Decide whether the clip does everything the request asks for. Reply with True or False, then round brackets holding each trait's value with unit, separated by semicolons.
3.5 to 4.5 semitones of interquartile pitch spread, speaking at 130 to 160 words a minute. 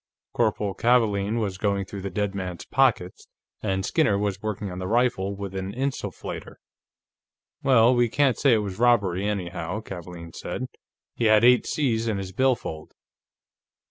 True (3.8 semitones; 155 wpm)